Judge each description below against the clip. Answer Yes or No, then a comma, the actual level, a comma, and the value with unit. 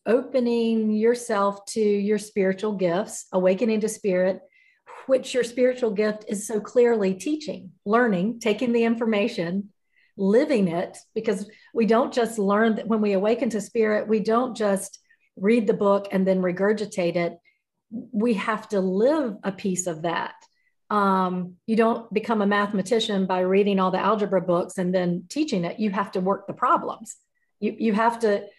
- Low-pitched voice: No, high, 210 Hz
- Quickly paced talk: No, average, 165 wpm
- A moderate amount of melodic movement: Yes, average, 3.1 semitones